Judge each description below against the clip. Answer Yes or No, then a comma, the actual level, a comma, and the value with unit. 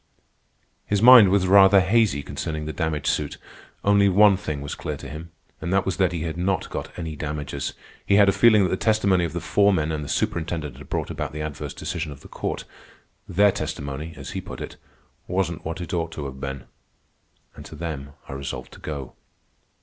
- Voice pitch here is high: No, very low, 85 Hz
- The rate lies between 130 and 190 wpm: No, fast, 205 wpm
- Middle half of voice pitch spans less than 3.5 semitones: No, average, 4.4 semitones